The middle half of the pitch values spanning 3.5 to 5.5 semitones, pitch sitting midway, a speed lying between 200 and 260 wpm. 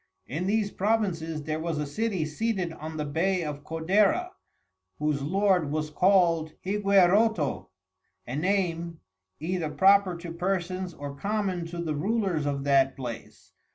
No: average, 4.2 semitones; medium, 170 Hz; average, 140 wpm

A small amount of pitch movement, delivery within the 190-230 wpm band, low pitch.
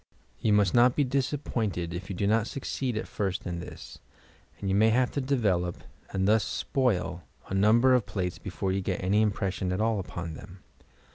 No: average, 4.2 semitones; average, 195 wpm; low, 100 Hz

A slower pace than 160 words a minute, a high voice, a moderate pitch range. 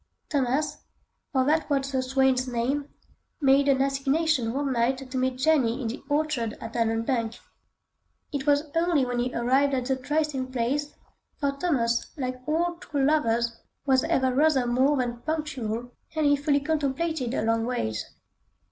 Yes: average, 150 wpm; very high, 265 Hz; average, 3.0 semitones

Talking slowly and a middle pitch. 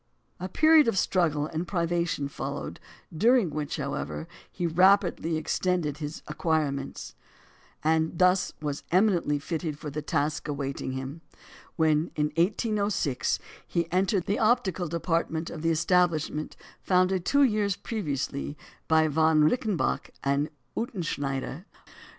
Yes: slow, 120 wpm; medium, 165 Hz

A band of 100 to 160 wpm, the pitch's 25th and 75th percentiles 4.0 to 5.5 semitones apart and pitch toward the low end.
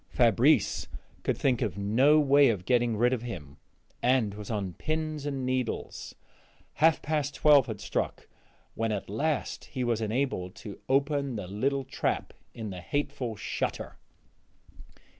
Yes: average, 145 wpm; average, 4.9 semitones; low, 125 Hz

